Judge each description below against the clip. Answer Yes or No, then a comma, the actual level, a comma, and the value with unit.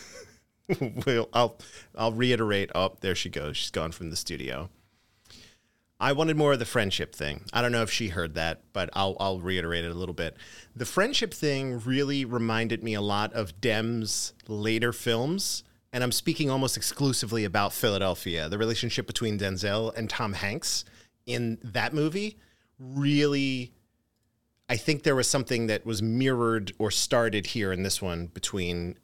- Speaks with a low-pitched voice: Yes, low, 115 Hz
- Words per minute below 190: Yes, average, 165 wpm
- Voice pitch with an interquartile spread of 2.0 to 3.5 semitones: No, average, 4.3 semitones